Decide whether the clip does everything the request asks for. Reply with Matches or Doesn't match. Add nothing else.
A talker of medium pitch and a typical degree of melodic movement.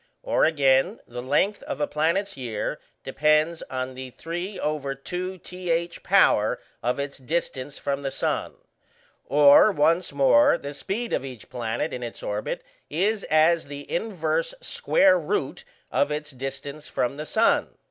Matches